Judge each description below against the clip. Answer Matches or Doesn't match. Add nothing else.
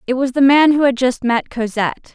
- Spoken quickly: Matches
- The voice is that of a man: Doesn't match